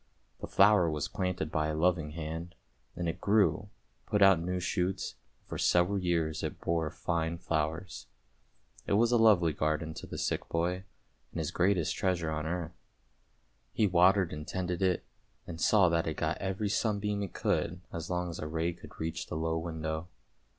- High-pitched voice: No, very low, 85 Hz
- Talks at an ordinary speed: Yes, average, 180 wpm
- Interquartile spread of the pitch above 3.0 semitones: No, average, 2.7 semitones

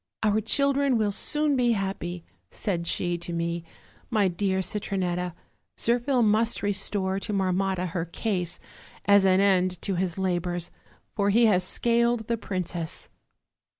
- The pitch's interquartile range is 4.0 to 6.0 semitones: No, average, 3.6 semitones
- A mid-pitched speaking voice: No, high, 195 Hz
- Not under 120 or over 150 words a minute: Yes, average, 145 wpm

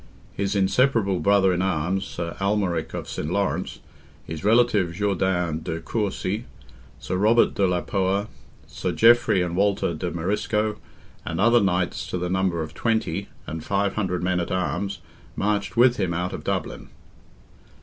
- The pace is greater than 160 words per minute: No, average, 155 wpm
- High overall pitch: No, very low, 95 Hz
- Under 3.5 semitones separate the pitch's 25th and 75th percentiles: Yes, narrow, 2.6 semitones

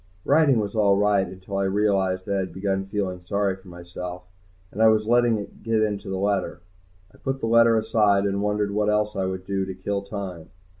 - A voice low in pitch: Yes, low, 100 Hz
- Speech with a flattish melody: Yes, narrow, 1.9 semitones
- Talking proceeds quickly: Yes, fast, 215 wpm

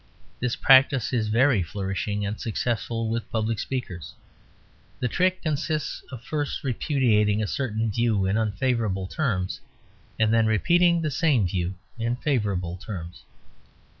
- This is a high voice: No, low, 115 Hz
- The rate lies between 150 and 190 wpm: No, slow, 135 wpm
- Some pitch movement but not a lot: Yes, average, 4.5 semitones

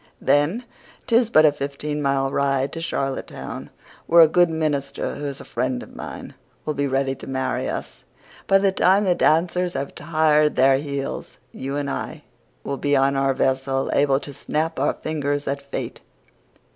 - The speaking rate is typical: Yes, average, 175 wpm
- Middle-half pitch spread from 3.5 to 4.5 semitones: No, narrow, 2.6 semitones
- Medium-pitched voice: Yes, medium, 145 Hz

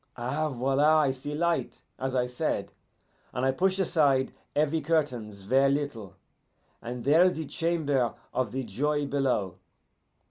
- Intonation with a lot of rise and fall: No, average, 3.6 semitones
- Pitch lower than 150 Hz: Yes, low, 135 Hz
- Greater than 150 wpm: No, average, 145 wpm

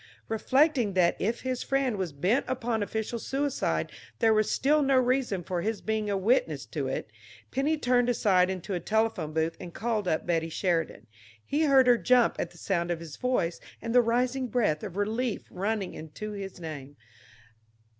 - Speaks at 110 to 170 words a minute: No, average, 180 wpm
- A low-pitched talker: No, high, 220 Hz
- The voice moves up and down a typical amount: No, wide, 5.8 semitones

